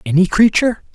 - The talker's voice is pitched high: Yes, high, 195 Hz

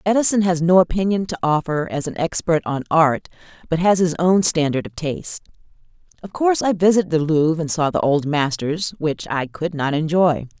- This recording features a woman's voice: Yes, female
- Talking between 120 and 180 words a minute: No, average, 190 wpm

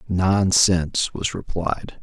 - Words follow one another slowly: Yes, slow, 90 wpm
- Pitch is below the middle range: Yes, very low, 90 Hz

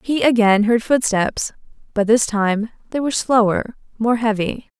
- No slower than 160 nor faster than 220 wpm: No, average, 150 wpm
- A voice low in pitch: No, high, 225 Hz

